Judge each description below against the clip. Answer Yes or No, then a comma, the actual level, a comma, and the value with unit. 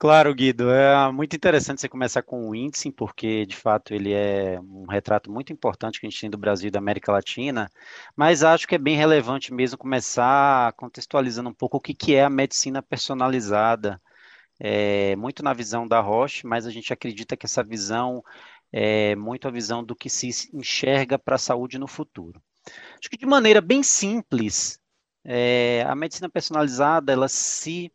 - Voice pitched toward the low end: Yes, low, 125 Hz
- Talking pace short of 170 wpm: No, average, 180 wpm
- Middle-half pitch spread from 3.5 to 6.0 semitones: Yes, average, 4.3 semitones